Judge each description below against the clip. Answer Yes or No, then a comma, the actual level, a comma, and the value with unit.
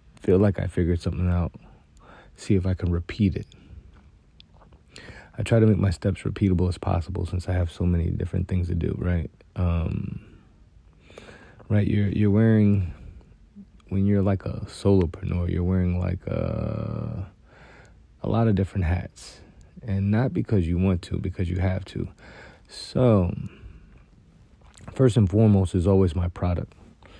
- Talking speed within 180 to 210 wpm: No, average, 150 wpm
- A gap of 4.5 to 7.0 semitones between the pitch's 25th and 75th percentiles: No, narrow, 2.6 semitones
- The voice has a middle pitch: No, very low, 95 Hz